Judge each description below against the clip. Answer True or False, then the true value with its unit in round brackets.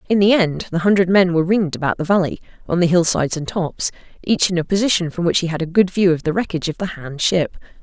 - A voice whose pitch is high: False (175 Hz)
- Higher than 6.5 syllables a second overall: True (6.7 syllables/s)